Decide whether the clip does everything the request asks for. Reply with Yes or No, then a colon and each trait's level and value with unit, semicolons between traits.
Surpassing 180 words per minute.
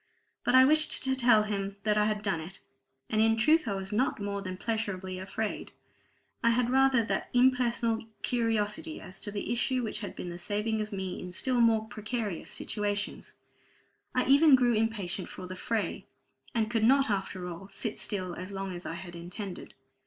Yes: average, 190 wpm